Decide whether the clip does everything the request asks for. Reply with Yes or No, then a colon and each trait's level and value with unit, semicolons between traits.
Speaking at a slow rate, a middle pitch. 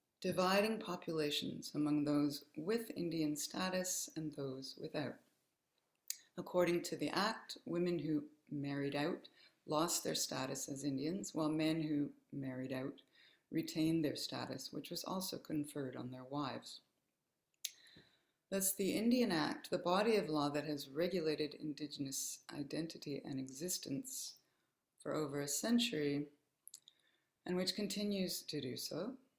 Yes: slow, 130 wpm; medium, 155 Hz